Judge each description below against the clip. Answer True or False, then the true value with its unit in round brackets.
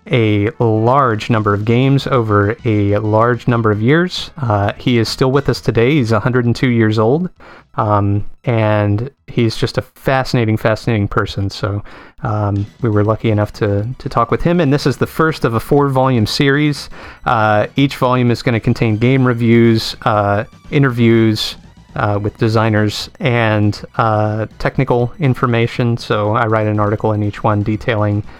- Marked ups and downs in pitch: False (3.4 semitones)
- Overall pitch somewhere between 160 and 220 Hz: False (115 Hz)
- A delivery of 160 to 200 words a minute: True (165 wpm)